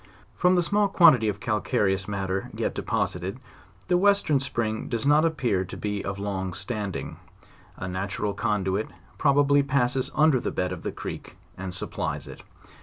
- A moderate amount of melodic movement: No, wide, 6.7 semitones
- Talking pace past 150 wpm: Yes, average, 165 wpm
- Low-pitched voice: Yes, low, 110 Hz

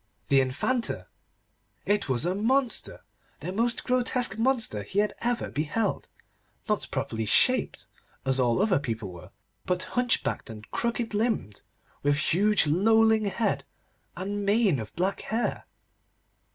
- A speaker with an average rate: No, slow, 130 wpm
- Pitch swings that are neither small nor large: No, wide, 8.2 semitones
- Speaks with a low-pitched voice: No, high, 200 Hz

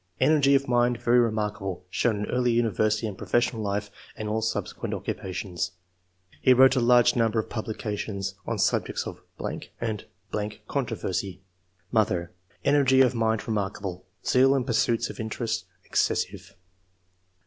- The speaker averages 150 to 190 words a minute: No, average, 140 wpm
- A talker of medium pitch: No, low, 110 Hz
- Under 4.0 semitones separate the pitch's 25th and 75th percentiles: Yes, average, 3.0 semitones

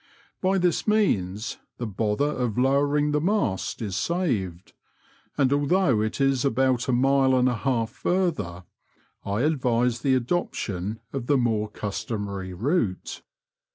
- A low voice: Yes, low, 125 Hz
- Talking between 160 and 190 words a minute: No, slow, 135 wpm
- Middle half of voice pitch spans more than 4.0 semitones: Yes, average, 5.3 semitones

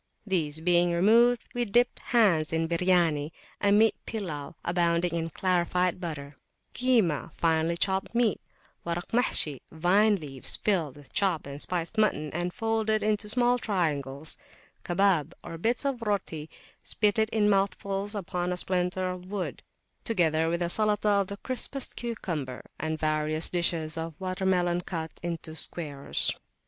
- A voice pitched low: No, medium, 180 Hz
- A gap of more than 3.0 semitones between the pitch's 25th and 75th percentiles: Yes, average, 4.3 semitones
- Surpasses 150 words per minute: No, average, 145 wpm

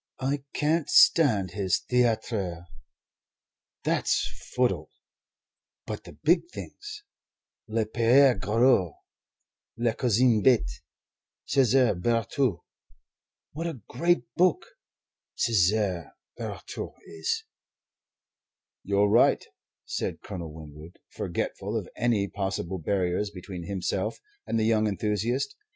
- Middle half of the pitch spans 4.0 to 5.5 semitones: Yes, average, 5.1 semitones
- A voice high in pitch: No, low, 110 Hz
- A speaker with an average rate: No, slow, 100 wpm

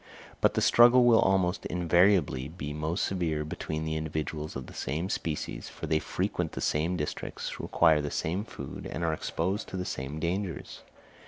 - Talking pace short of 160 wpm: No, average, 175 wpm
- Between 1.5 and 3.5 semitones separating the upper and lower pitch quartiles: Yes, average, 3.2 semitones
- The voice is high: No, very low, 80 Hz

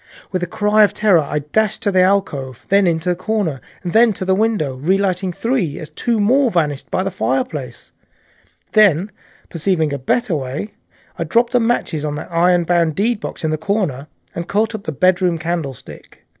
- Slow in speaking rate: No, average, 185 wpm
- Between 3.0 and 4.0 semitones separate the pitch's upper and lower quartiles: No, average, 4.9 semitones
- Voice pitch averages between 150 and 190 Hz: Yes, medium, 185 Hz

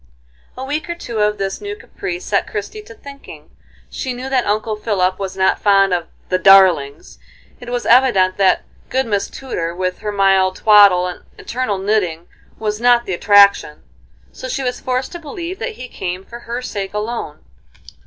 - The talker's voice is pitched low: No, high, 210 Hz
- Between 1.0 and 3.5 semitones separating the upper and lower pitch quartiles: No, average, 5.2 semitones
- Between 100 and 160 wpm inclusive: No, average, 180 wpm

